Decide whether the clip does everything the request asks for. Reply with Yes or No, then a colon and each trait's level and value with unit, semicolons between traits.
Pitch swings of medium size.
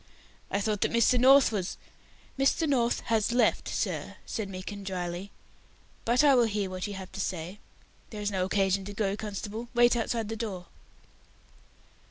Yes: average, 3.4 semitones